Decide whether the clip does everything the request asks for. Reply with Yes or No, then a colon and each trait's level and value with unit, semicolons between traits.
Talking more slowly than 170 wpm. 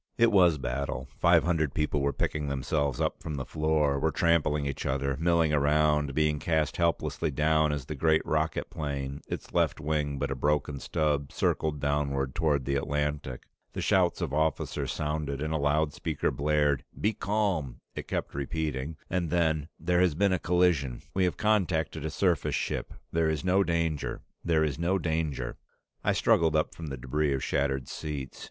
No: average, 180 wpm